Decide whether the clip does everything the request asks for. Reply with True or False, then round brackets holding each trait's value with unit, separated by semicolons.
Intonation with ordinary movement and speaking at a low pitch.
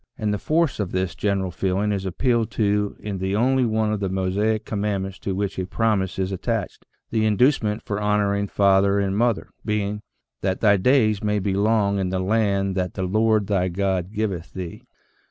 False (2.1 semitones; 100 Hz)